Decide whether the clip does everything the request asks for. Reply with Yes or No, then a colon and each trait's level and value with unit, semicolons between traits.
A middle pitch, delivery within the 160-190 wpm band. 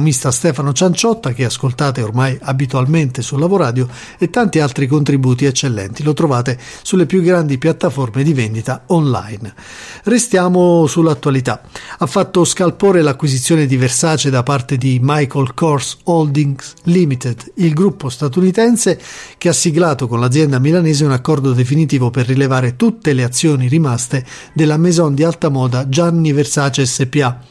No: medium, 145 Hz; average, 140 wpm